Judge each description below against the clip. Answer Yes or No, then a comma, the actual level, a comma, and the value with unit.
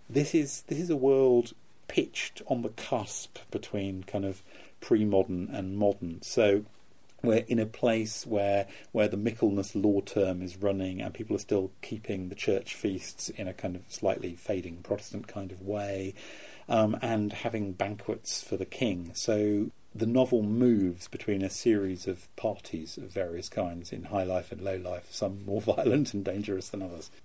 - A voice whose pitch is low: Yes, low, 100 Hz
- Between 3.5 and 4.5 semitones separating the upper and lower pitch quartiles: No, average, 2.8 semitones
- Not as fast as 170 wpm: No, average, 175 wpm